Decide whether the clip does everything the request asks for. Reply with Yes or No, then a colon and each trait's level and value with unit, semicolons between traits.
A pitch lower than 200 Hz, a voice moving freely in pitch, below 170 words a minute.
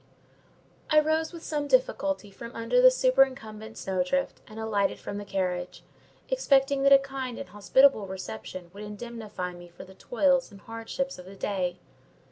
No: high, 225 Hz; wide, 6.1 semitones; average, 160 wpm